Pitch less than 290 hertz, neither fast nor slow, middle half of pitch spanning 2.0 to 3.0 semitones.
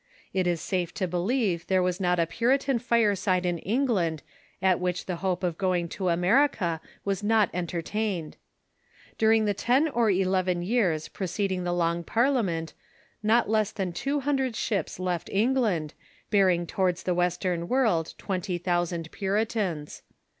No: medium, 185 Hz; average, 150 wpm; average, 3.9 semitones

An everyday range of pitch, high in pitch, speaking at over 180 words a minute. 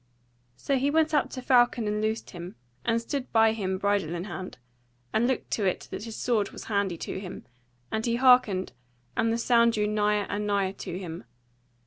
Yes: average, 3.4 semitones; high, 215 Hz; average, 195 wpm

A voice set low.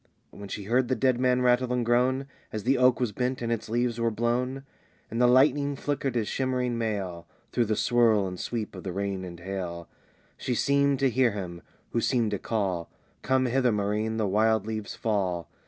Yes: low, 115 Hz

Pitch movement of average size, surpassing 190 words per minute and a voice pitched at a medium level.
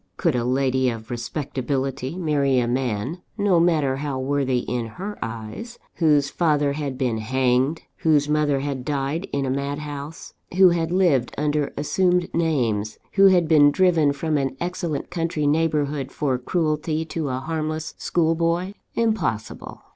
No: average, 3.8 semitones; average, 150 wpm; medium, 145 Hz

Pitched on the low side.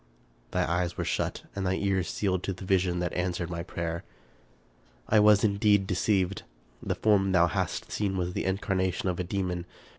Yes: very low, 95 Hz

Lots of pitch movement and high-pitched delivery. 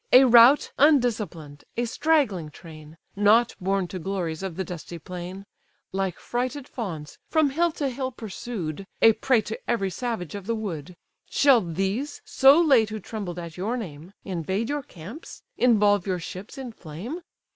Yes: wide, 5.7 semitones; high, 205 Hz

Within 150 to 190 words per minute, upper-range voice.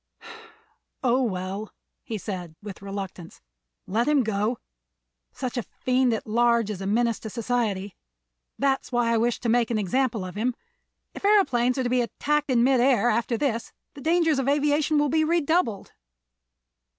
Yes: average, 170 wpm; high, 240 Hz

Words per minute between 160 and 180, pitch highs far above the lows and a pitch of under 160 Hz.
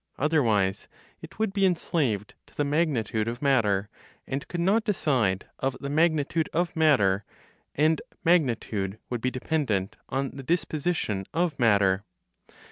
No: slow, 135 wpm; wide, 7.2 semitones; medium, 140 Hz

